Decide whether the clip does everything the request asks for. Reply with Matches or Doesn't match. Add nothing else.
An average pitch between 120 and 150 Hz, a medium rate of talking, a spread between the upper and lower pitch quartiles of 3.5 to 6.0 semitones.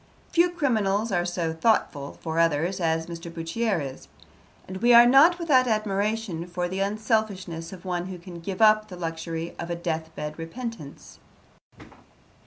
Doesn't match